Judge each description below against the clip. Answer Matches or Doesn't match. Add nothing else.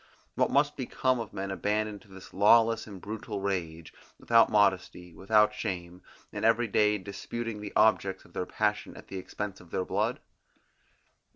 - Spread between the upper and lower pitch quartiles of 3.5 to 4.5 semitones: Doesn't match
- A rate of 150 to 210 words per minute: Matches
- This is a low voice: Matches